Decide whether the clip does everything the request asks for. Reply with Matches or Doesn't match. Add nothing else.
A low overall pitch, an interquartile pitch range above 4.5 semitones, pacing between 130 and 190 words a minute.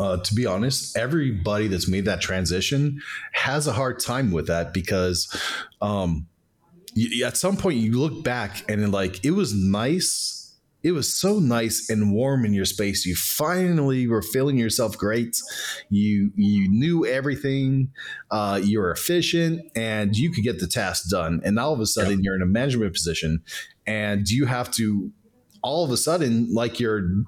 Matches